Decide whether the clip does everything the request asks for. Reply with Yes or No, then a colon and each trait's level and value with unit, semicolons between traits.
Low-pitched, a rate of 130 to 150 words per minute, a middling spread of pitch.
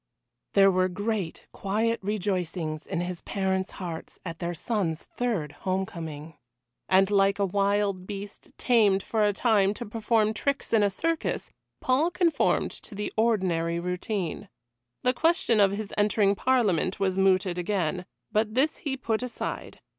No: high, 200 Hz; average, 145 wpm; average, 3.2 semitones